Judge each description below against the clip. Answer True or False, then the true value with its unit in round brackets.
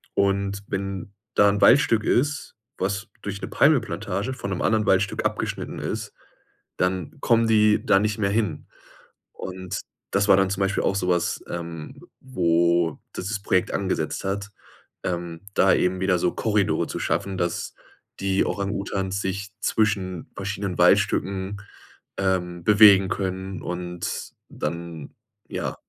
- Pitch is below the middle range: True (95 Hz)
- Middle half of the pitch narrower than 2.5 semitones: True (2.0 semitones)